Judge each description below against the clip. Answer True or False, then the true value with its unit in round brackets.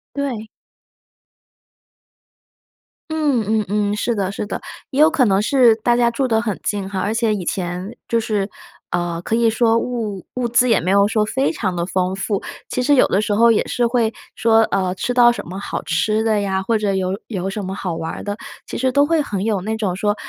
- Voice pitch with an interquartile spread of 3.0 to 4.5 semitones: True (3.6 semitones)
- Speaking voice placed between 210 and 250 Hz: True (215 Hz)